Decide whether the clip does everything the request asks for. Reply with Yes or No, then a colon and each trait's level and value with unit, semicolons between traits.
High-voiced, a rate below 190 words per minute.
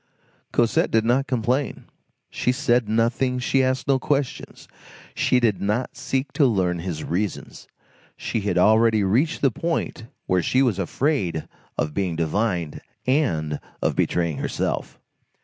No: low, 115 Hz; average, 140 wpm